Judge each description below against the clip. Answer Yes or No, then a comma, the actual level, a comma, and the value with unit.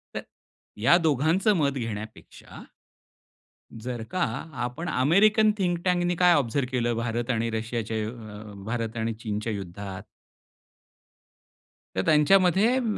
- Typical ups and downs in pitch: No, wide, 7.9 semitones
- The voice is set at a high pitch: No, low, 120 Hz